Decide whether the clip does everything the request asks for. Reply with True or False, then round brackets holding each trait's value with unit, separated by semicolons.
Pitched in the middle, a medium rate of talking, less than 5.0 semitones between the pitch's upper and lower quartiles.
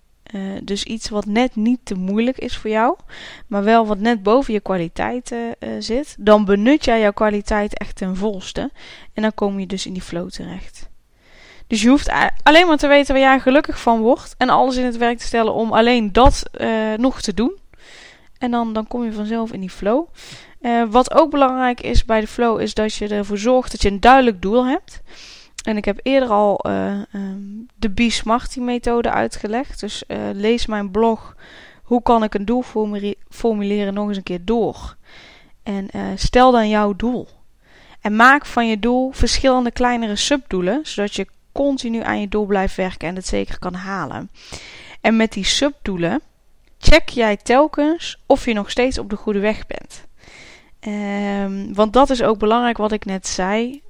False (225 Hz; 190 wpm; 3.3 semitones)